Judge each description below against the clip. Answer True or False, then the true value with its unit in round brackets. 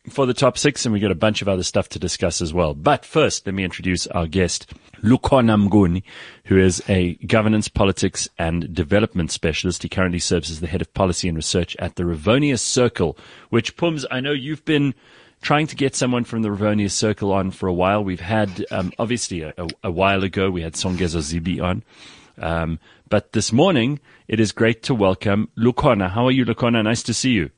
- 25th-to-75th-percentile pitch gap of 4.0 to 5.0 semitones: True (4.5 semitones)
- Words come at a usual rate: False (210 wpm)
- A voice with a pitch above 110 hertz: False (100 Hz)